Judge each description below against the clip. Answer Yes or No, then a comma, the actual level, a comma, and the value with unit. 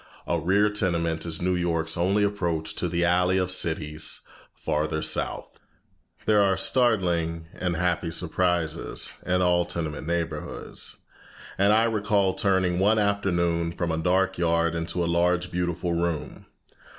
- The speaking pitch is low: Yes, very low, 90 Hz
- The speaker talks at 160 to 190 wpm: No, average, 140 wpm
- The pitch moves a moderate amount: No, narrow, 2.2 semitones